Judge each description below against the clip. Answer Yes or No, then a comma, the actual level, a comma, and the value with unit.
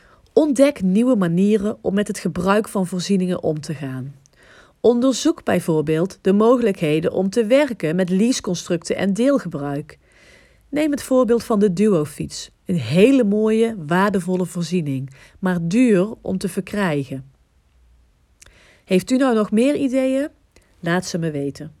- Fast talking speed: No, slow, 135 wpm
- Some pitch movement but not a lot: No, wide, 6.2 semitones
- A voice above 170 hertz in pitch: Yes, medium, 185 Hz